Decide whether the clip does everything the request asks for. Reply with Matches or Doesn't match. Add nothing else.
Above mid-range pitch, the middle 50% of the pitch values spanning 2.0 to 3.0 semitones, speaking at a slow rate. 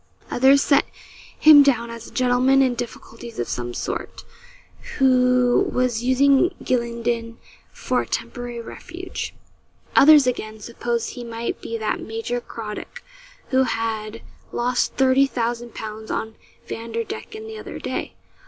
Matches